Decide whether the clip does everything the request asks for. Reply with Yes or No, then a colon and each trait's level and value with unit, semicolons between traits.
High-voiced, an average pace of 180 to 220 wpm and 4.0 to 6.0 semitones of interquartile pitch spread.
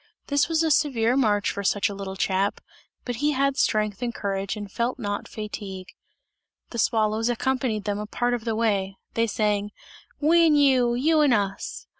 Yes: high, 225 Hz; average, 185 wpm; average, 4.3 semitones